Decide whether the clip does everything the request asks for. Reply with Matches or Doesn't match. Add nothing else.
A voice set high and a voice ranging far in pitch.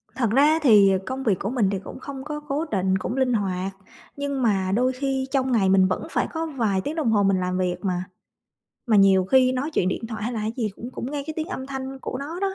Matches